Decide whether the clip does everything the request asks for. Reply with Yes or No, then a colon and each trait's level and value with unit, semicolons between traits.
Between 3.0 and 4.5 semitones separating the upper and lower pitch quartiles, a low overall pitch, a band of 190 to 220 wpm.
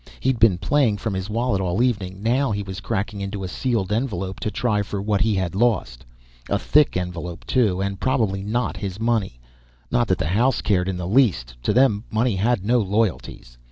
Yes: average, 3.8 semitones; low, 100 Hz; fast, 205 wpm